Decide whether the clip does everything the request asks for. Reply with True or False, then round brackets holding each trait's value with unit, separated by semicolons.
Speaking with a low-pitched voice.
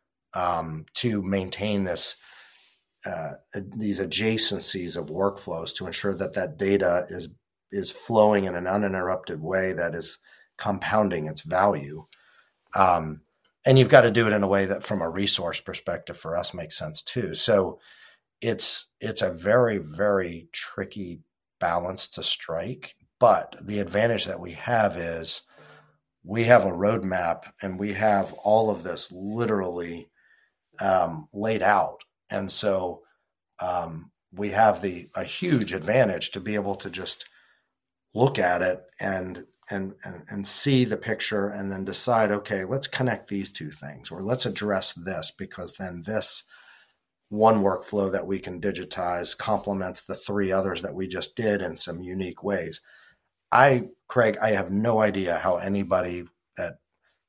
True (100 Hz)